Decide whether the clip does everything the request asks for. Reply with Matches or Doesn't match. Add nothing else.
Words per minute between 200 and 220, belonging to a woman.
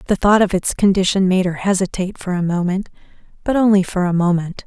Matches